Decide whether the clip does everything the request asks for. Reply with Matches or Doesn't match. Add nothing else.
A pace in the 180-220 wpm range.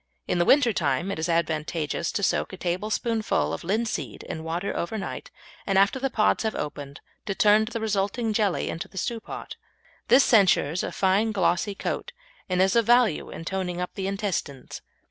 Matches